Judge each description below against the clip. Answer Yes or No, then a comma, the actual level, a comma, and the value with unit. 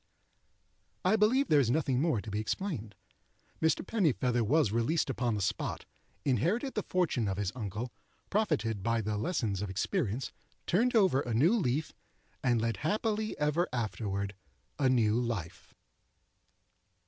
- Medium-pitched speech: No, low, 125 Hz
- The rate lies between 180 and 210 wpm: No, average, 145 wpm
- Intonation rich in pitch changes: Yes, wide, 8.0 semitones